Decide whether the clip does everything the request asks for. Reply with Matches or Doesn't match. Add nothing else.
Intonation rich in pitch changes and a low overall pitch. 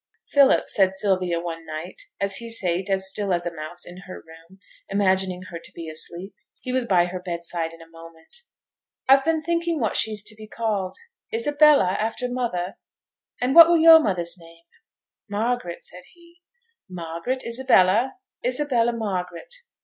Doesn't match